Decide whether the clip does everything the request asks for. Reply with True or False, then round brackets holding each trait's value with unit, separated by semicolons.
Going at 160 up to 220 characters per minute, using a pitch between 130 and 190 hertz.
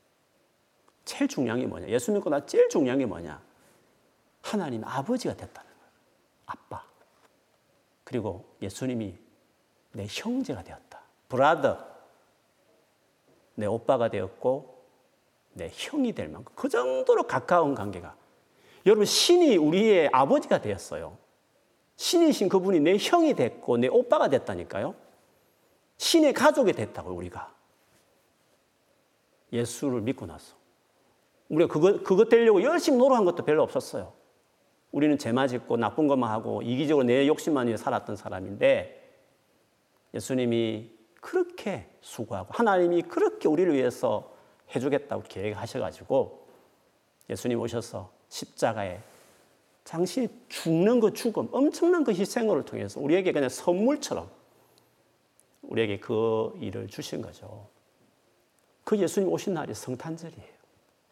False (275 characters per minute; 185 Hz)